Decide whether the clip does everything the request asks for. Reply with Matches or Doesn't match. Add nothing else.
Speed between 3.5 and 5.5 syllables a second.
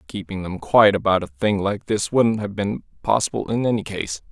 Matches